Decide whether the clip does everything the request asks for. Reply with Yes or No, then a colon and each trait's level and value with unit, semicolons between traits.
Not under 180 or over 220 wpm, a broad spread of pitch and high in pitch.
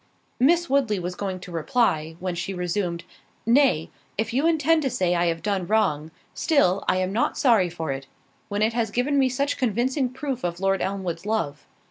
Yes: average, 190 wpm; wide, 6.4 semitones; high, 205 Hz